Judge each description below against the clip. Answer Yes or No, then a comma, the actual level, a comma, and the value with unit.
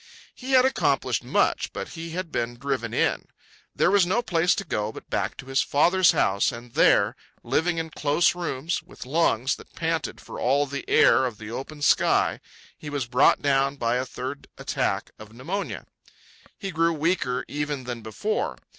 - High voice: No, medium, 145 Hz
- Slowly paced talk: No, average, 180 wpm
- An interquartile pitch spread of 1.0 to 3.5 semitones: No, average, 5.1 semitones